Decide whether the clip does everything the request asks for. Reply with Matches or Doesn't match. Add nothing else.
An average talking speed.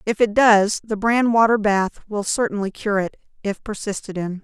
Matches